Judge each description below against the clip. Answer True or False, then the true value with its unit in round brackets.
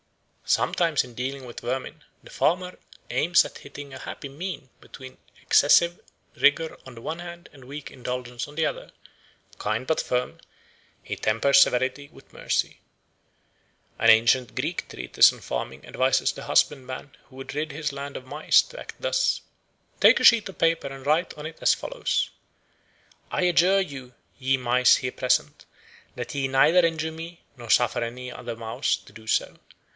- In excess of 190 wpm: False (165 wpm)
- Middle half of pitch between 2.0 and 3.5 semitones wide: False (4.3 semitones)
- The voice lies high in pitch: False (135 Hz)